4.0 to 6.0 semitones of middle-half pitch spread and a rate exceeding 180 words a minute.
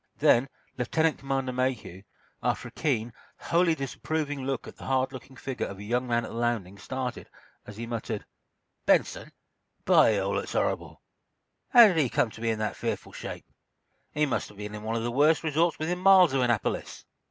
Yes: average, 4.8 semitones; average, 190 wpm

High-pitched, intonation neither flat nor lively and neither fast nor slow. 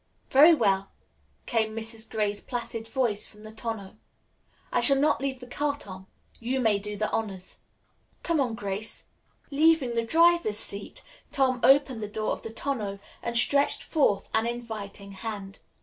Yes: high, 225 Hz; average, 4.2 semitones; average, 160 wpm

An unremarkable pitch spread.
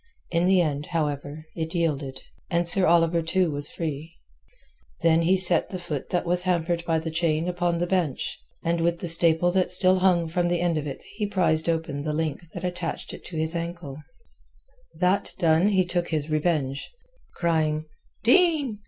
No: narrow, 2.1 semitones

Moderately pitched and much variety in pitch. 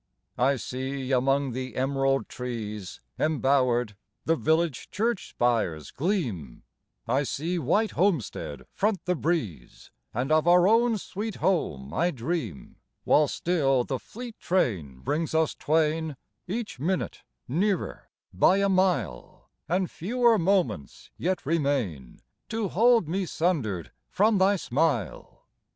Yes: medium, 155 Hz; wide, 7.0 semitones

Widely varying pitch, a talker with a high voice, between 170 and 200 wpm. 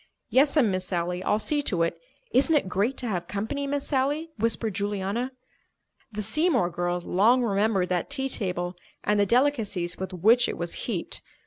Yes: wide, 6.2 semitones; high, 210 Hz; average, 175 wpm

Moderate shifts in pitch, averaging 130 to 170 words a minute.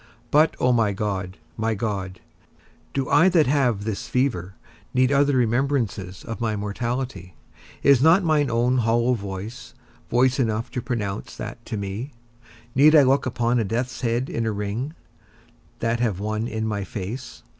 Yes: average, 3.8 semitones; average, 160 wpm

